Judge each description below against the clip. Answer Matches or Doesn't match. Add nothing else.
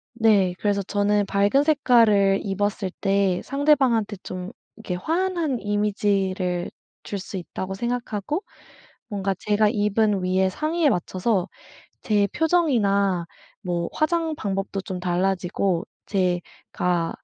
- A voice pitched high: Matches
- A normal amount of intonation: Matches